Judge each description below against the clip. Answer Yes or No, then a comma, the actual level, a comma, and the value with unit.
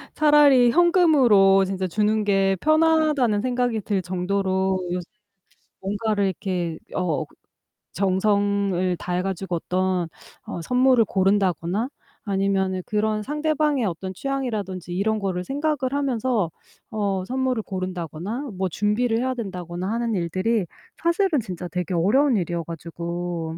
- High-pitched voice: Yes, high, 200 Hz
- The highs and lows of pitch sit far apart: No, average, 5.0 semitones